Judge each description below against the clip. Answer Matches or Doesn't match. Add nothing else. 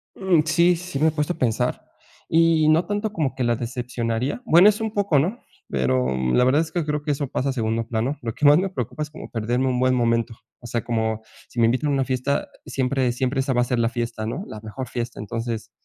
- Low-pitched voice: Matches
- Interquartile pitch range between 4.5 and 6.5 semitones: Matches